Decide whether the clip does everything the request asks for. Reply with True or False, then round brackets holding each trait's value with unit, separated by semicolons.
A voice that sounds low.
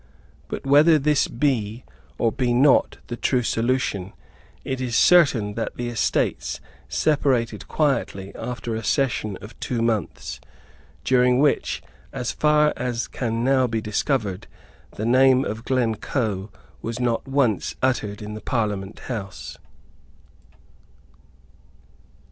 True (120 Hz)